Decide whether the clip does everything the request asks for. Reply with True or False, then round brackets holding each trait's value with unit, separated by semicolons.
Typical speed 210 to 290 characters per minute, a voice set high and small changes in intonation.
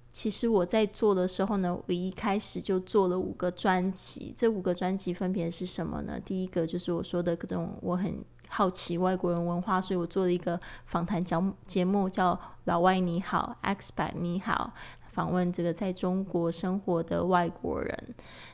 False (275 characters per minute; 180 Hz; 1.8 semitones)